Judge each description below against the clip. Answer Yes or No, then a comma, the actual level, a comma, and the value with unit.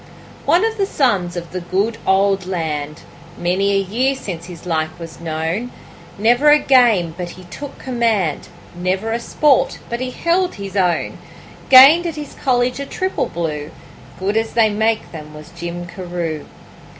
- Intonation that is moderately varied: No, wide, 6.2 semitones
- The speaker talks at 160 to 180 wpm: Yes, average, 165 wpm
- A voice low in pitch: No, high, 195 Hz